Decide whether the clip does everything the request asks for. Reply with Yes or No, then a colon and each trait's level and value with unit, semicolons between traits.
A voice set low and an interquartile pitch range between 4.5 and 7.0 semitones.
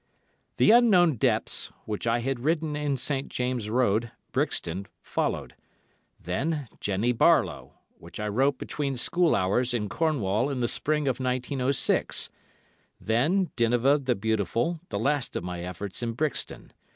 Yes: low, 125 Hz; average, 4.9 semitones